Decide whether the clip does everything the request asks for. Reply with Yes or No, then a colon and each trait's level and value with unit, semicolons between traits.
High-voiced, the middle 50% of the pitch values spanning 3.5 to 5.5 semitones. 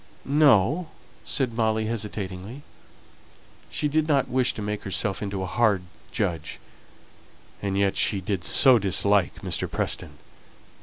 No: low, 105 Hz; average, 5.0 semitones